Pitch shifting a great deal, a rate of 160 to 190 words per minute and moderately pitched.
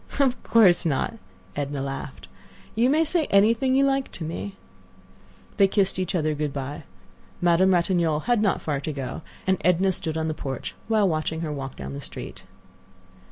Yes: wide, 5.7 semitones; average, 180 wpm; medium, 170 Hz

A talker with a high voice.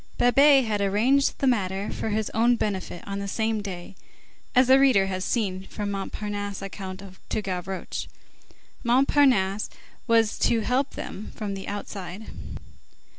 Yes: high, 210 Hz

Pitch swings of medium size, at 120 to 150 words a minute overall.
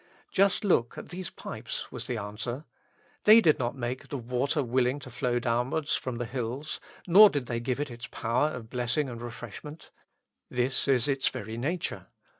No: average, 3.5 semitones; average, 180 wpm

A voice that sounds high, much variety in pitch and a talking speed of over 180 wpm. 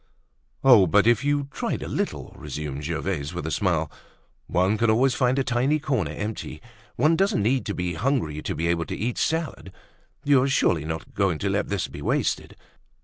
No: low, 105 Hz; wide, 7.7 semitones; average, 190 wpm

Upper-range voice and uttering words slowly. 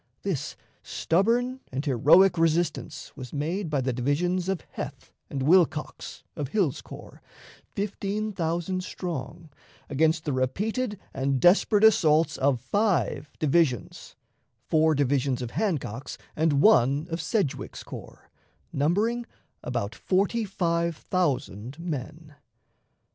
No: medium, 160 Hz; slow, 115 wpm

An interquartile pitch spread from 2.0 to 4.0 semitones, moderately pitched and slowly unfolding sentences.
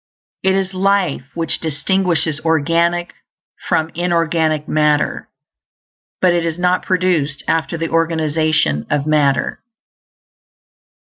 Yes: narrow, 2.4 semitones; medium, 165 Hz; slow, 105 wpm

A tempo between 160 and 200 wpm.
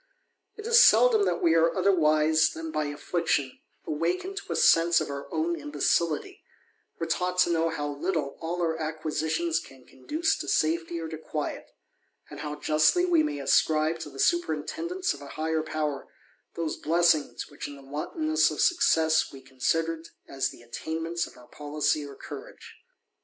Yes: average, 170 wpm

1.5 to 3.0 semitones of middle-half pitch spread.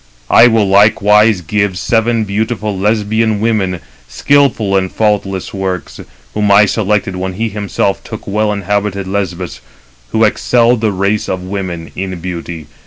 Yes: narrow, 2.5 semitones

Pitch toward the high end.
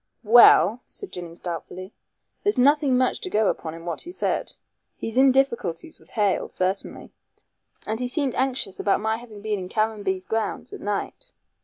Yes: high, 220 Hz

